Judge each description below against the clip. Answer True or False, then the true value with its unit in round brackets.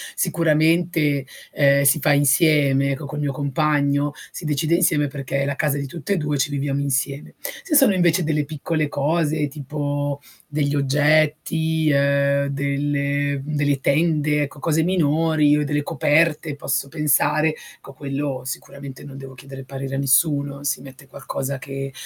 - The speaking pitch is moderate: True (145 Hz)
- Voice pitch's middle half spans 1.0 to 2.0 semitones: True (1.7 semitones)